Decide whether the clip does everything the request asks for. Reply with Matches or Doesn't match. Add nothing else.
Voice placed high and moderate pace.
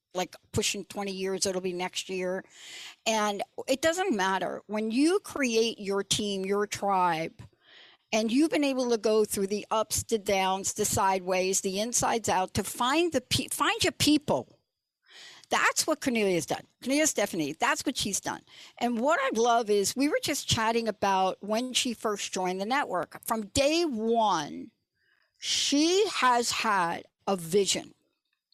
Matches